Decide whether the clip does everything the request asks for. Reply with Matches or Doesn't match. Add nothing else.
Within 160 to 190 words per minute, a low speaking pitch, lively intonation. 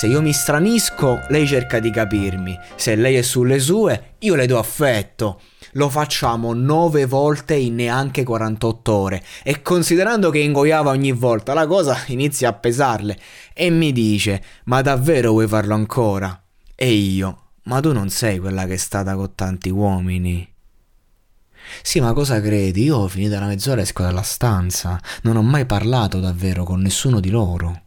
Matches